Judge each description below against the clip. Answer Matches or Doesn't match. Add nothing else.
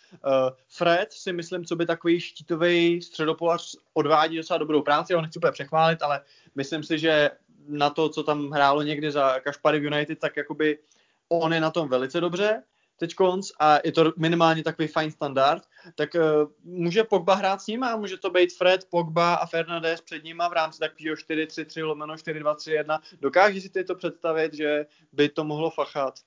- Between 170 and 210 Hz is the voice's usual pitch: Doesn't match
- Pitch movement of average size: Doesn't match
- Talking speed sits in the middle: Doesn't match